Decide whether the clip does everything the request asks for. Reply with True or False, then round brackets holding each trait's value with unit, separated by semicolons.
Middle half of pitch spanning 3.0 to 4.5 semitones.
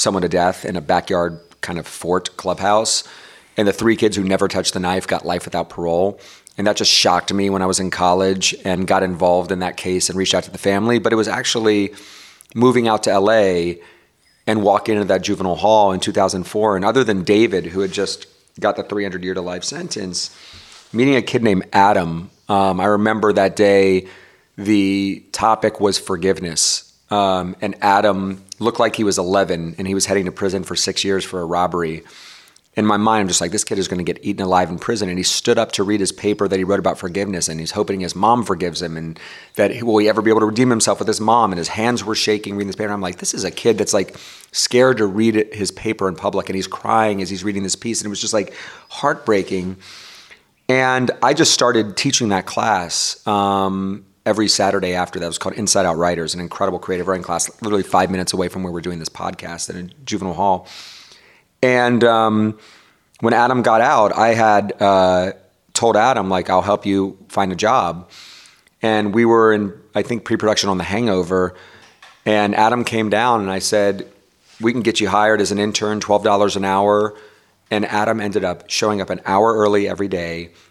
False (2.6 semitones)